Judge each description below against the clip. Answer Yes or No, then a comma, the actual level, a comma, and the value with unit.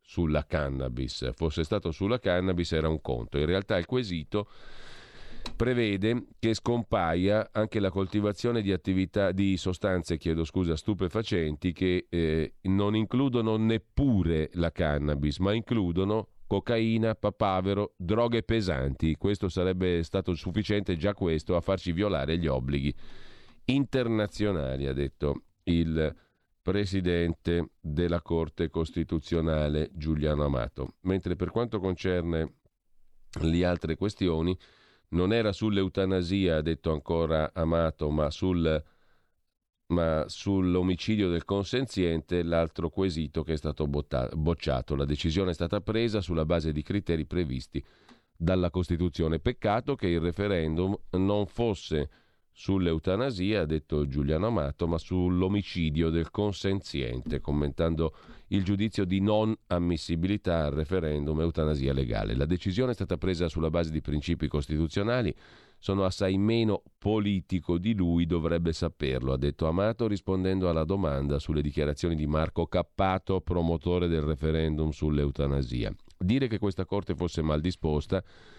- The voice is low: Yes, very low, 90 Hz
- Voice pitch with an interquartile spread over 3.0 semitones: Yes, average, 4.0 semitones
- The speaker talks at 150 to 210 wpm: No, average, 125 wpm